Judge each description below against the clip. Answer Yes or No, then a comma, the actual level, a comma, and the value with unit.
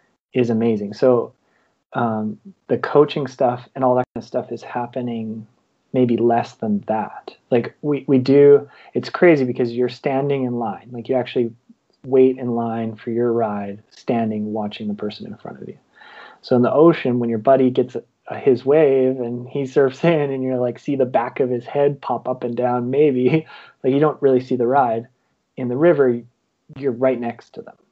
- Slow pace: No, average, 200 wpm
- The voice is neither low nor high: No, low, 125 Hz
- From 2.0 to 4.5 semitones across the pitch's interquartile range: Yes, narrow, 2.4 semitones